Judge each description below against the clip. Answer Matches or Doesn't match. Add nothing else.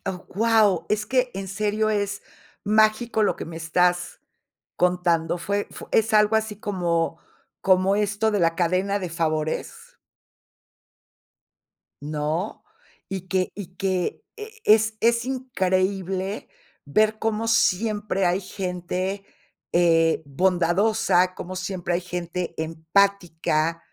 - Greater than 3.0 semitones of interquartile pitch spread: Matches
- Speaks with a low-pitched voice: Doesn't match